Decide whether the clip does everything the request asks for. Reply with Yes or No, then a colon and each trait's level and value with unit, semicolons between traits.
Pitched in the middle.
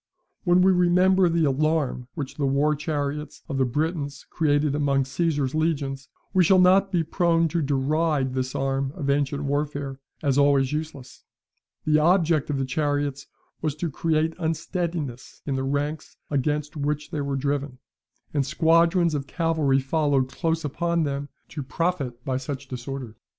Yes: medium, 145 Hz